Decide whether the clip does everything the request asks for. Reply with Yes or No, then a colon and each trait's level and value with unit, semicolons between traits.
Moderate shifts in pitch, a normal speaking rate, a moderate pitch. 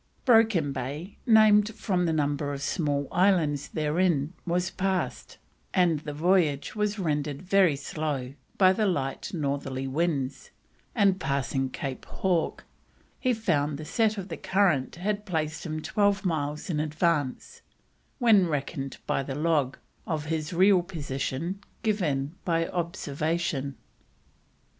No: average, 4.8 semitones; slow, 130 wpm; medium, 160 Hz